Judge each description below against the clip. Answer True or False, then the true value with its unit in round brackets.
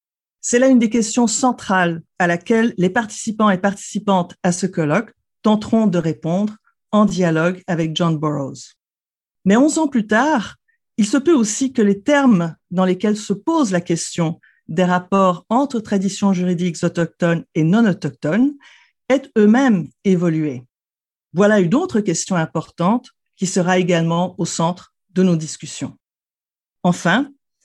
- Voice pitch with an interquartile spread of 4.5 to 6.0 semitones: True (4.8 semitones)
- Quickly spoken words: False (145 wpm)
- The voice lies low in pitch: False (195 Hz)